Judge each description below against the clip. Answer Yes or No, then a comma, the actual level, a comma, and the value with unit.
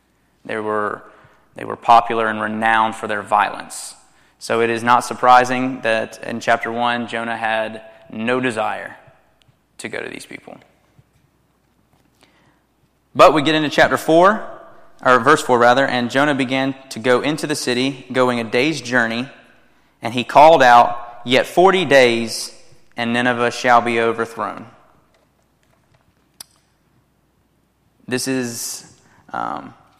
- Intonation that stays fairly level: Yes, narrow, 1.9 semitones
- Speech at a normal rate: No, slow, 130 wpm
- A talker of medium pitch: No, low, 120 Hz